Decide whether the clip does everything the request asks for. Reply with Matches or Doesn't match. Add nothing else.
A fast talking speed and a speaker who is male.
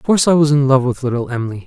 Matches